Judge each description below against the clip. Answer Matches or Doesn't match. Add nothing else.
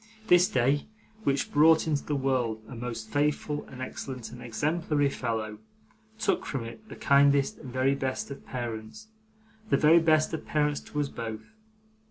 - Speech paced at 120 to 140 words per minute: Doesn't match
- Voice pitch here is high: Doesn't match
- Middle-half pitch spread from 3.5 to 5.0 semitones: Matches